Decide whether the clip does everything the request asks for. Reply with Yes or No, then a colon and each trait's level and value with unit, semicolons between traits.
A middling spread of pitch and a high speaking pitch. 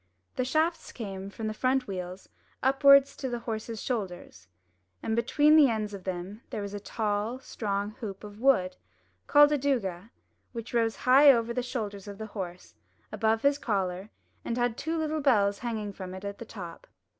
Yes: average, 4.3 semitones; high, 220 Hz